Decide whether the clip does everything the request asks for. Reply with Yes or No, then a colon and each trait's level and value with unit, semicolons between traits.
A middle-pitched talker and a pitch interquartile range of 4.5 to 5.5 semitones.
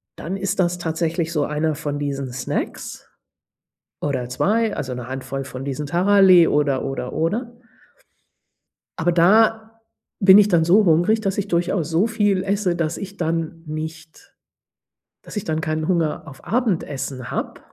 Yes: medium, 165 Hz; average, 4.8 semitones